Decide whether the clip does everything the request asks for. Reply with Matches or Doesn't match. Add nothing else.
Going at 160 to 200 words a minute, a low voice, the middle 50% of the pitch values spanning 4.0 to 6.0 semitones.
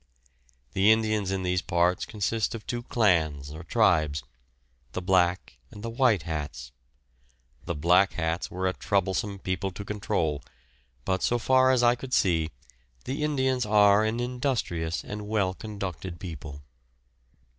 Doesn't match